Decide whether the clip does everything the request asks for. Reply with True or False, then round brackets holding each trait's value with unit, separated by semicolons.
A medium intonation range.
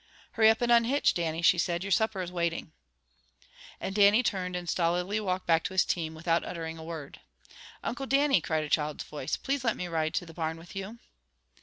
True (4.4 semitones)